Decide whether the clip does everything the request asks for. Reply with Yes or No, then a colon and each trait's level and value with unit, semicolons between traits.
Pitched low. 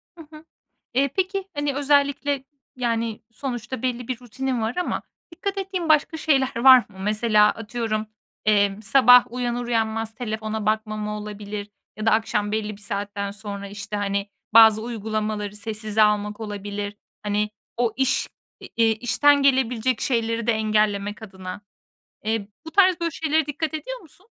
No: high, 225 Hz